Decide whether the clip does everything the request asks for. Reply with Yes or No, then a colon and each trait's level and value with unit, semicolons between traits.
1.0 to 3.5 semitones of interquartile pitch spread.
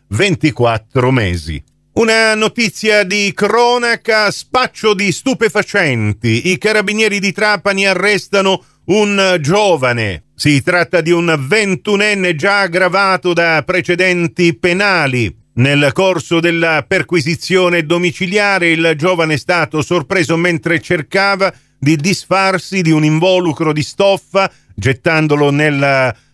No: average, 4.3 semitones